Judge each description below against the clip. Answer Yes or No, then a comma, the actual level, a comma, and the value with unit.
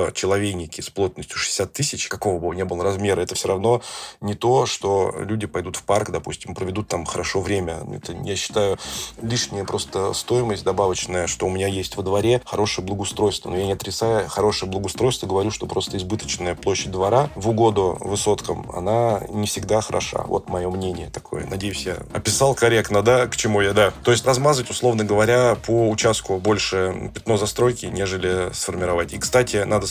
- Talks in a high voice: No, low, 100 Hz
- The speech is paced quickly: Yes, fast, 175 wpm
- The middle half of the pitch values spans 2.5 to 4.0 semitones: Yes, average, 3.2 semitones